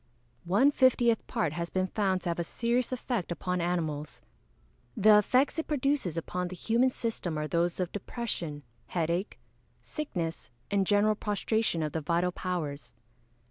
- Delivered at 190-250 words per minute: No, average, 155 wpm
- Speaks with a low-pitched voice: No, medium, 185 Hz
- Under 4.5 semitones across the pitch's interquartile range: No, average, 5.3 semitones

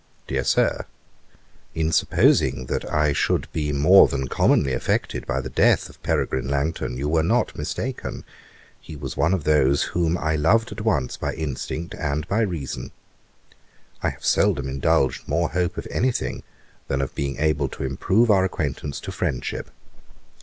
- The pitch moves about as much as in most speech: Yes, average, 4.0 semitones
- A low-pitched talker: Yes, very low, 75 Hz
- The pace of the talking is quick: No, average, 165 wpm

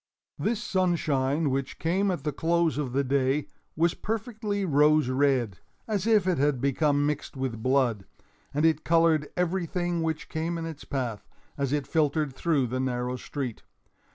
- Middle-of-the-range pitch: Yes, medium, 150 Hz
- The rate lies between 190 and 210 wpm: No, average, 155 wpm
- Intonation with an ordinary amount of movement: Yes, average, 4.1 semitones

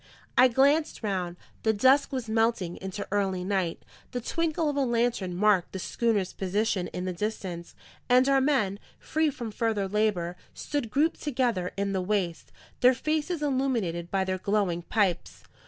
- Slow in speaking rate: No, average, 160 wpm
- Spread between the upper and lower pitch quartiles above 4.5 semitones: Yes, wide, 5.6 semitones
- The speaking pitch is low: No, high, 215 Hz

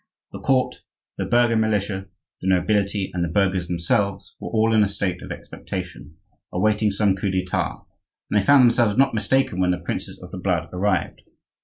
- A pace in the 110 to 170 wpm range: No, average, 180 wpm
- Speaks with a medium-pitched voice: No, low, 100 Hz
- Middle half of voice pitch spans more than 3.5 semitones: No, average, 3.1 semitones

